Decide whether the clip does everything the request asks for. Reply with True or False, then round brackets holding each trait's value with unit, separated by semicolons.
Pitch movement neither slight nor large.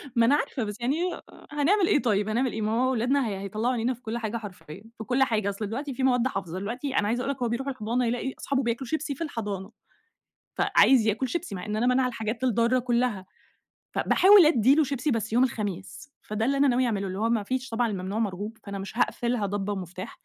True (3.7 semitones)